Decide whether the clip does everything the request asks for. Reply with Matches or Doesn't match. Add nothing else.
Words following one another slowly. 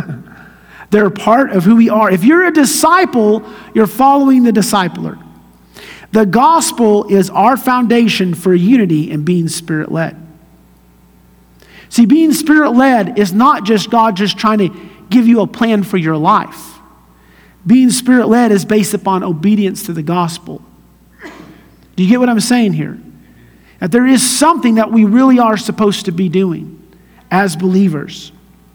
Doesn't match